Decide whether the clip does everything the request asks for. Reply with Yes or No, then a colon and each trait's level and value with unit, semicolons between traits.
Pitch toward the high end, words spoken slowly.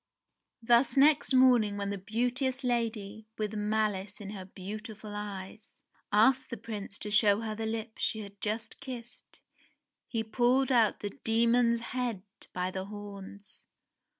No: high, 220 Hz; average, 145 wpm